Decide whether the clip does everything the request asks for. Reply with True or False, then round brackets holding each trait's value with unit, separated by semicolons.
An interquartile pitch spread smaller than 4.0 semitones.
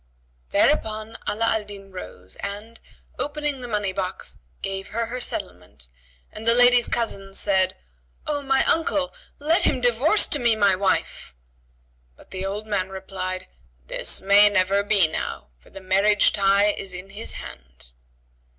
True (3.4 semitones)